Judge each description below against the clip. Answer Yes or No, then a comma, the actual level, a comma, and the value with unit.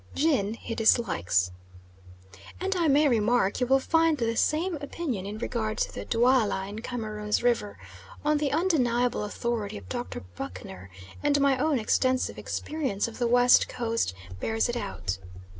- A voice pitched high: Yes, high, 240 Hz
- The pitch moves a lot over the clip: No, average, 4.8 semitones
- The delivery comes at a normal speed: Yes, average, 155 wpm